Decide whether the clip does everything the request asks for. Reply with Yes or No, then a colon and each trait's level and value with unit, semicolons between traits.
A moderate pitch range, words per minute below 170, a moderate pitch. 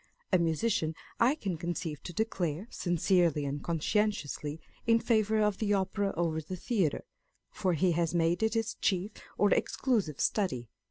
Yes: average, 4.6 semitones; average, 155 wpm; medium, 180 Hz